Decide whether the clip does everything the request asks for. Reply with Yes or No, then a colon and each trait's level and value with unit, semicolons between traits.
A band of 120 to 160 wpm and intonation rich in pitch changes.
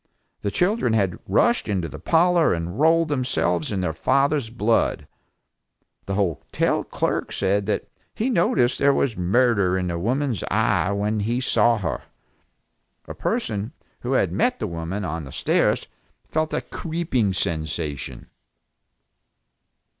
Yes: average, 140 wpm; wide, 7.2 semitones